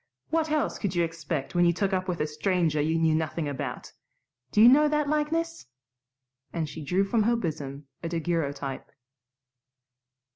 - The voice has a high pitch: No, medium, 170 Hz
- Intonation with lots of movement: Yes, wide, 6.6 semitones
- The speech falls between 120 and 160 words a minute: No, average, 170 wpm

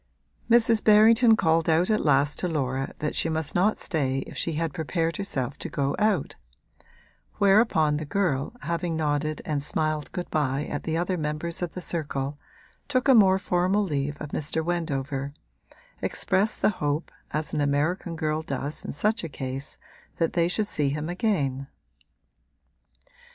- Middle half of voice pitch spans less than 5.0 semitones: Yes, average, 4.0 semitones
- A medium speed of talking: Yes, average, 160 wpm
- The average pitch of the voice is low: No, medium, 160 Hz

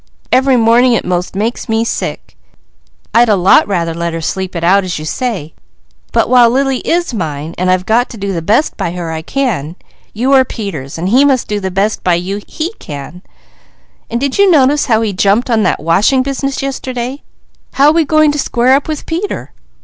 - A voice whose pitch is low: No, high, 225 Hz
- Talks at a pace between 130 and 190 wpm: No, fast, 205 wpm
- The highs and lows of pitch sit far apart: Yes, wide, 6.7 semitones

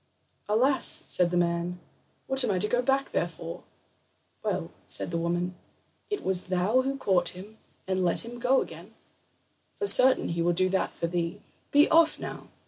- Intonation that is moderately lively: No, wide, 6.4 semitones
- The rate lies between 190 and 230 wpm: No, average, 180 wpm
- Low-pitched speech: No, high, 190 Hz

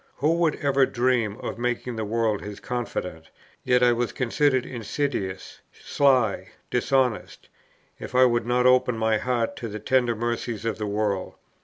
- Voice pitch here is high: No, low, 120 Hz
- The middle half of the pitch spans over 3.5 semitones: No, narrow, 2.6 semitones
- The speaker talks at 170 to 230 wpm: No, average, 160 wpm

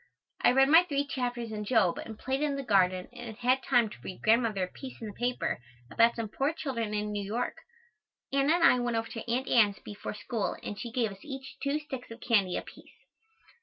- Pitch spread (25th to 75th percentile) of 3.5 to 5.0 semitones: Yes, average, 4.1 semitones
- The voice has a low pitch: No, high, 235 Hz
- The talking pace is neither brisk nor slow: No, fast, 220 wpm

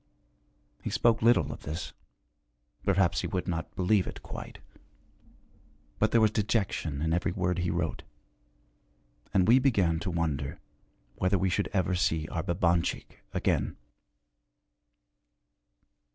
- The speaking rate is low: Yes, slow, 125 wpm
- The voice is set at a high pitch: No, very low, 90 Hz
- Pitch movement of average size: Yes, average, 3.3 semitones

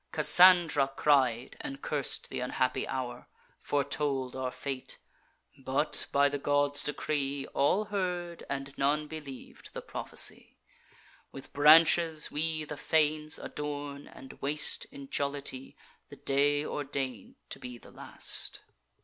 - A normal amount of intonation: No, narrow, 1.9 semitones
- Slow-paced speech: Yes, slow, 125 wpm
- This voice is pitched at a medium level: Yes, medium, 145 Hz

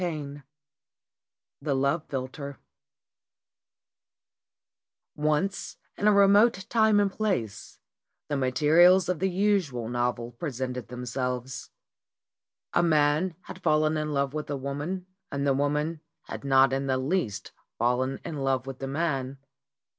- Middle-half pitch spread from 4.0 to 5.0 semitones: Yes, average, 4.6 semitones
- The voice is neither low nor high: Yes, medium, 145 Hz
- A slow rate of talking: Yes, slow, 130 wpm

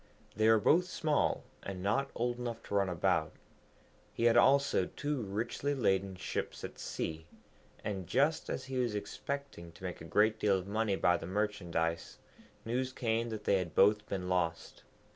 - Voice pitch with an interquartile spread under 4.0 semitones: No, average, 4.9 semitones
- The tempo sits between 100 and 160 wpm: No, average, 175 wpm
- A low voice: Yes, low, 105 Hz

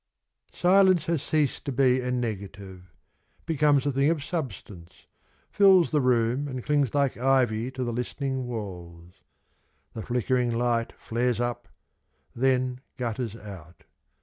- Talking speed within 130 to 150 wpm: Yes, average, 140 wpm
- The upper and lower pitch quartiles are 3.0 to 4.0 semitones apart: Yes, average, 3.6 semitones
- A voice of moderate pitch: No, low, 125 Hz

